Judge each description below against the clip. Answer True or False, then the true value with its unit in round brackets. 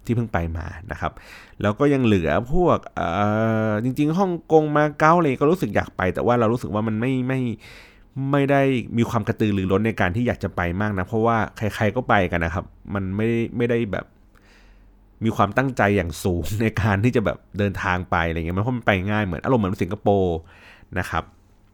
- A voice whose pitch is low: True (105 Hz)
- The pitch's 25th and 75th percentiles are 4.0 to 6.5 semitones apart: False (3.5 semitones)